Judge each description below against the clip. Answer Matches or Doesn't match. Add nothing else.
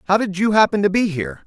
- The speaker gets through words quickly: Matches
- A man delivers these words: Matches